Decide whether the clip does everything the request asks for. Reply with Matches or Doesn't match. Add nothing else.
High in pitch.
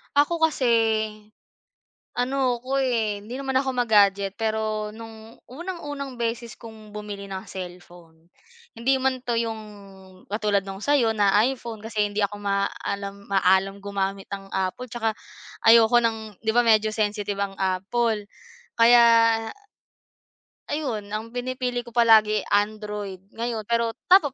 Matches